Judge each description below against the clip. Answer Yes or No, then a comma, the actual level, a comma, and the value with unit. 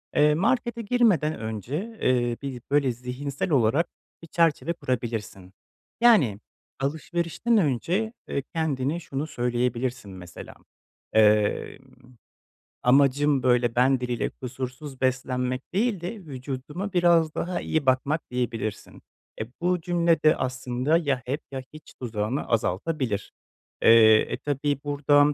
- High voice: No, low, 135 Hz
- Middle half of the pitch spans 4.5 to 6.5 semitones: Yes, average, 4.8 semitones